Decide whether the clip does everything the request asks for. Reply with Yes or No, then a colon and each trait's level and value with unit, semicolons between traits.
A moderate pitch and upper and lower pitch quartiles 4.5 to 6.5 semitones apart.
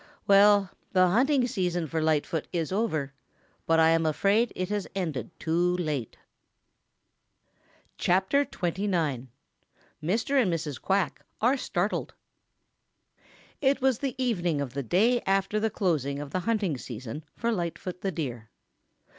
Yes: medium, 180 Hz; average, 5.1 semitones